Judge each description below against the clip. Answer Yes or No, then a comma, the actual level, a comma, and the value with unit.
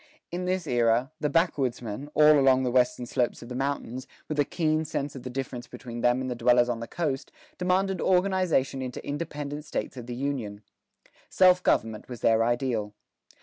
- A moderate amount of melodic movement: Yes, average, 3.9 semitones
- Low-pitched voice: Yes, low, 130 Hz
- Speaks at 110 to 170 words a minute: No, average, 185 wpm